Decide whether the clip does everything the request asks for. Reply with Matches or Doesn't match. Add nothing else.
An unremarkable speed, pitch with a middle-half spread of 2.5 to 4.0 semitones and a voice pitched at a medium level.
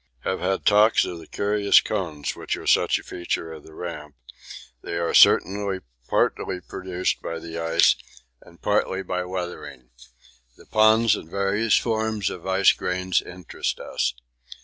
Doesn't match